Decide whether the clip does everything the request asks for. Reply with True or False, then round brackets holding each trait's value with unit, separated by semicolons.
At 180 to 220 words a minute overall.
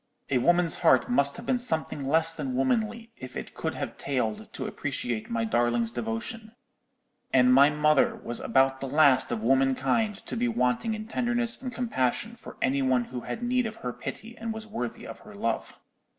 True (190 wpm)